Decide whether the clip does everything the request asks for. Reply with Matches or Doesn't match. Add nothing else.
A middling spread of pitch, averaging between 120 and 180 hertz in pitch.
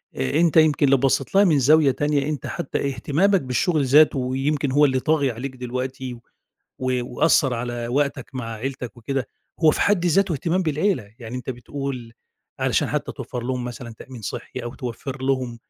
Matches